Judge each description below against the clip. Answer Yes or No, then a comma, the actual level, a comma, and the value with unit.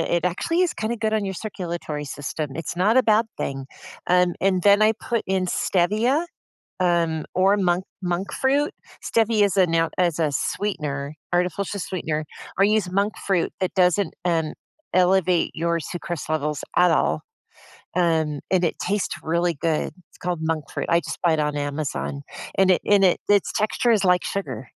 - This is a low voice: No, medium, 180 Hz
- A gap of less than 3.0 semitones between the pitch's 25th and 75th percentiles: No, average, 3.7 semitones